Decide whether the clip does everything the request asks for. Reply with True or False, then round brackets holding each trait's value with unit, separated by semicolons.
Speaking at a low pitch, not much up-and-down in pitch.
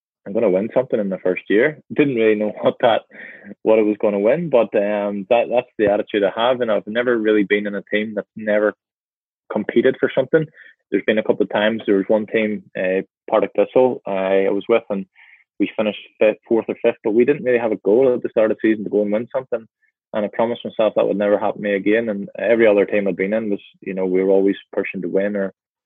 True (105 Hz; 2.2 semitones)